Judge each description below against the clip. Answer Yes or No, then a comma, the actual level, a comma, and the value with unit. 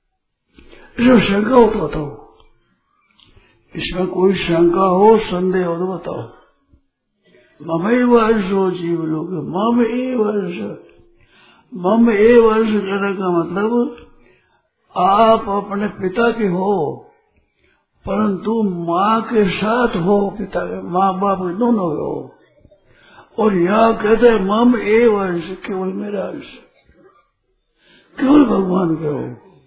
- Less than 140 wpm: Yes, average, 115 wpm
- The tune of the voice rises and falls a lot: No, average, 3.3 semitones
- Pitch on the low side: No, high, 200 Hz